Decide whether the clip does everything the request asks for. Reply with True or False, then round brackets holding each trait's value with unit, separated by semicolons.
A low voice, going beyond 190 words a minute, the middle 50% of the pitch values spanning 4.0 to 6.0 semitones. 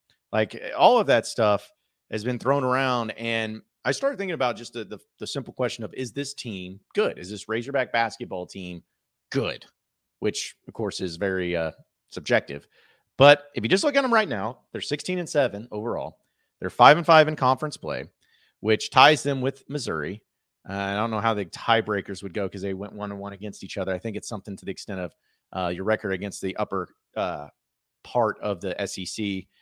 True (110 Hz; 205 wpm; 4.8 semitones)